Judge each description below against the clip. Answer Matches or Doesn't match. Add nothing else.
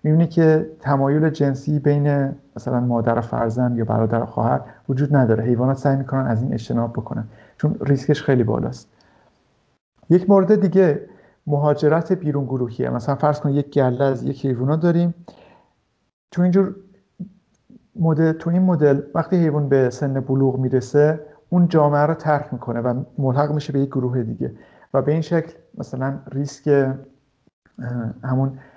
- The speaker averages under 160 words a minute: Matches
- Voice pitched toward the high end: Doesn't match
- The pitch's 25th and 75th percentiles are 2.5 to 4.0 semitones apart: Matches